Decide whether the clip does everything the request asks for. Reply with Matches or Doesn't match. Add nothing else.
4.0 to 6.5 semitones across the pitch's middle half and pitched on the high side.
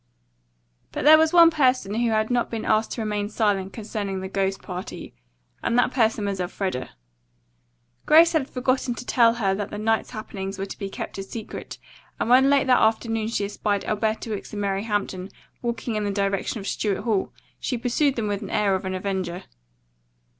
Doesn't match